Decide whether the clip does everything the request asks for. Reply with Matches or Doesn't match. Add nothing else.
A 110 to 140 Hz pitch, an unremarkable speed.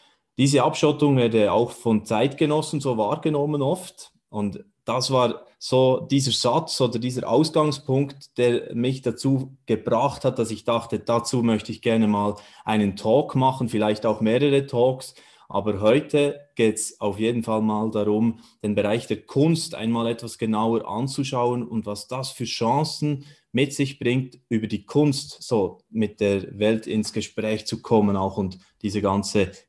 Matches